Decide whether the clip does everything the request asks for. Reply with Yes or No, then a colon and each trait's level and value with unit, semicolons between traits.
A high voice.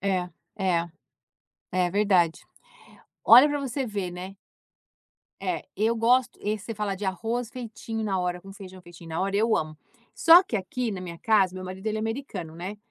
Yes: high, 200 Hz